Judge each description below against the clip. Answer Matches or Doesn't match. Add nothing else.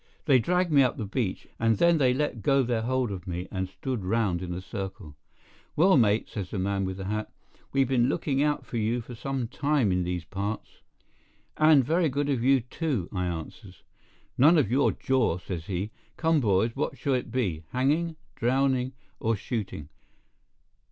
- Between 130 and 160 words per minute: Doesn't match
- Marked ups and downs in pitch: Matches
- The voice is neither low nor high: Doesn't match